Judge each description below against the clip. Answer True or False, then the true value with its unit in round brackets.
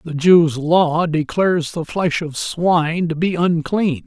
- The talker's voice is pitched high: False (165 Hz)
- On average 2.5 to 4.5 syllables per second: True (3.8 syllables/s)